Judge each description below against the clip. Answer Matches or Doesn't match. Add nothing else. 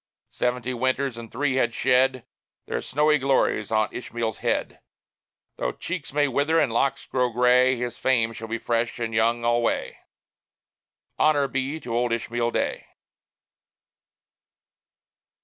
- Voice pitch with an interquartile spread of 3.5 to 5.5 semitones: Doesn't match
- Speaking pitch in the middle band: Doesn't match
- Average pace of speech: Doesn't match